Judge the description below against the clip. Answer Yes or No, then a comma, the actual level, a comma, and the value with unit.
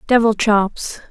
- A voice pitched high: Yes, high, 215 Hz